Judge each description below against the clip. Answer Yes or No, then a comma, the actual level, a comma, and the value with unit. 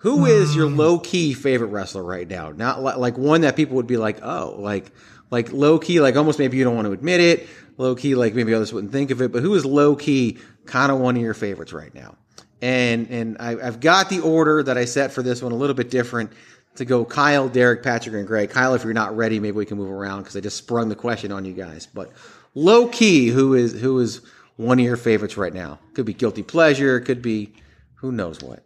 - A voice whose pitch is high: No, low, 120 Hz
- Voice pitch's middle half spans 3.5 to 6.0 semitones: Yes, average, 4.2 semitones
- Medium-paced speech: No, fast, 250 wpm